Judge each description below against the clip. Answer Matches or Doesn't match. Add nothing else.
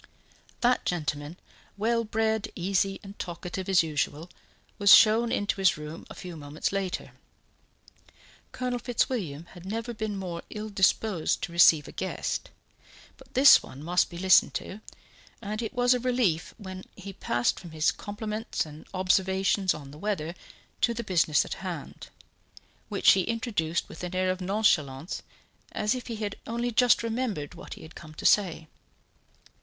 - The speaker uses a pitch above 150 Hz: Matches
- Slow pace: Doesn't match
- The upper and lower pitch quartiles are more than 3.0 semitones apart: Matches